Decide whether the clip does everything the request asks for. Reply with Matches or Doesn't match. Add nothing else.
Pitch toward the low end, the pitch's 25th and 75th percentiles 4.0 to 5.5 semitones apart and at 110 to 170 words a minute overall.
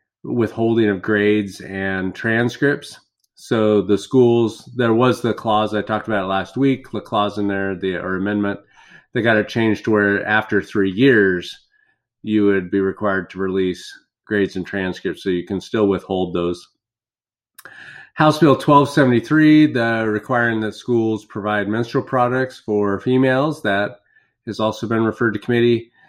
Doesn't match